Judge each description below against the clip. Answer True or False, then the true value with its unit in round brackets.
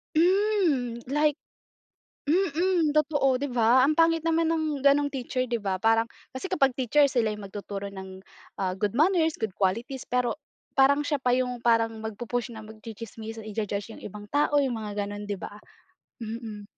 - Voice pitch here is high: True (245 Hz)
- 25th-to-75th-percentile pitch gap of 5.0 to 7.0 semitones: True (5.3 semitones)